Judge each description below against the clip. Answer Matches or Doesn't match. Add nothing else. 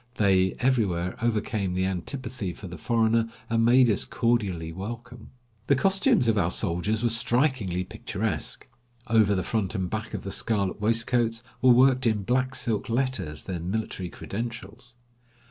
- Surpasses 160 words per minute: Doesn't match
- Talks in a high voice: Doesn't match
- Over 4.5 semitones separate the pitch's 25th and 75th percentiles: Doesn't match